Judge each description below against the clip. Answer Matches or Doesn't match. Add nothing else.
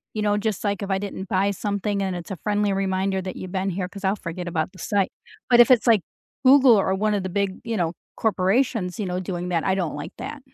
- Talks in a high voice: Matches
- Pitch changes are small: Matches